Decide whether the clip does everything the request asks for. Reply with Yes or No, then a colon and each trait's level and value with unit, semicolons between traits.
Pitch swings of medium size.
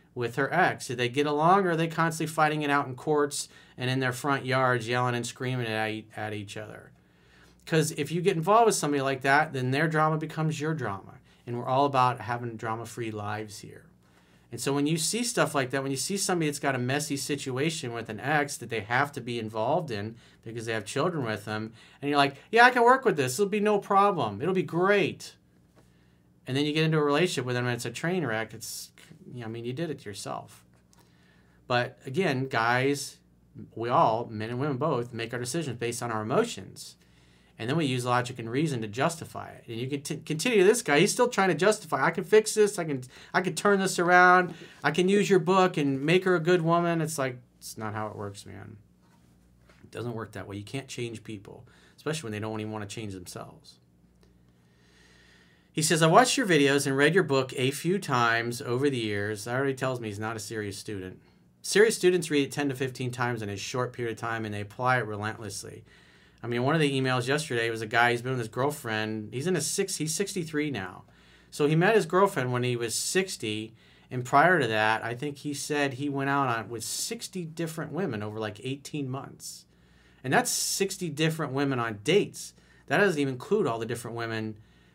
No: wide, 6.1 semitones